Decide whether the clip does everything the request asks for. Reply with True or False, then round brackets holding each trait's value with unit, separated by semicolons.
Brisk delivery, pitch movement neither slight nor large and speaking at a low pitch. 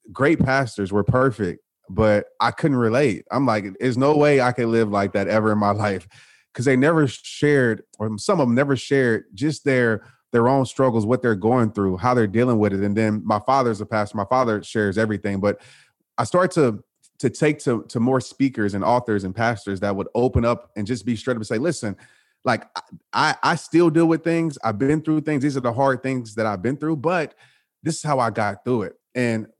True (225 wpm; 4.2 semitones; 120 Hz)